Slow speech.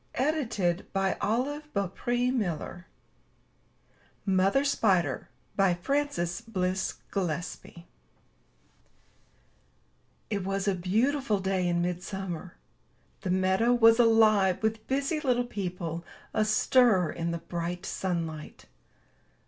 Yes: slow, 90 wpm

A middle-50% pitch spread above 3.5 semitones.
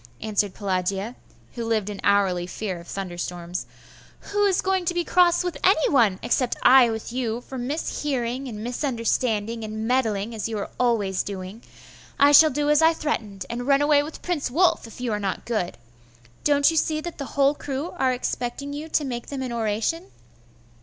Yes: wide, 5.6 semitones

